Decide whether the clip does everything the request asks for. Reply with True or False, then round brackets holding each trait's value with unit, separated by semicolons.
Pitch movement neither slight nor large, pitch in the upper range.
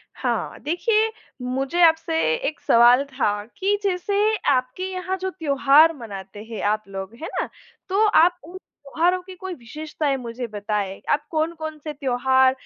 False (6.3 semitones; 295 Hz)